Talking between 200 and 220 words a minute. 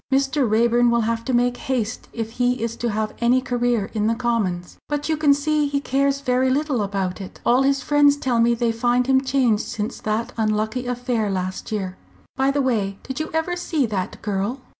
Yes: fast, 205 wpm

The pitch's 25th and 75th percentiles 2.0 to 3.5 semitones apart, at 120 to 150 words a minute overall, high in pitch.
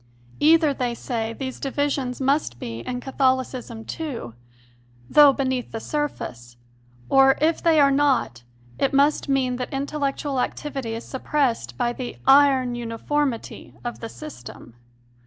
Yes: average, 3.1 semitones; slow, 135 wpm; very high, 265 Hz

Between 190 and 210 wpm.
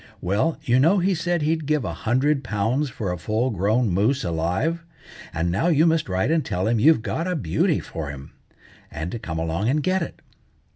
Yes: fast, 205 wpm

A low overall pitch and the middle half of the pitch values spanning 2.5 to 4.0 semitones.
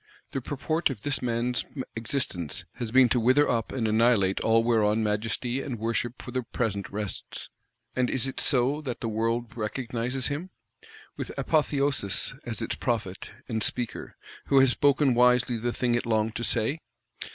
Yes: low, 120 Hz; average, 2.8 semitones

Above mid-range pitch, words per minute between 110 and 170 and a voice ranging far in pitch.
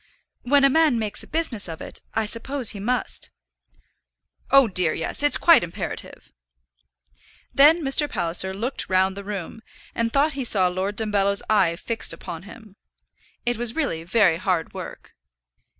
Yes: high, 215 Hz; average, 155 wpm; wide, 5.9 semitones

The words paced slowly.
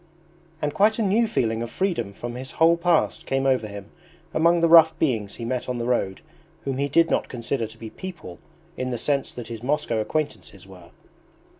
No: average, 200 wpm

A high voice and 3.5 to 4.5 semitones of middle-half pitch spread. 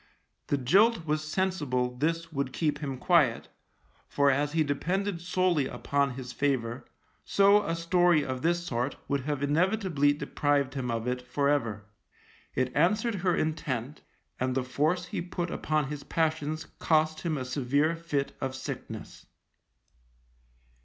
No: medium, 150 Hz; average, 4.1 semitones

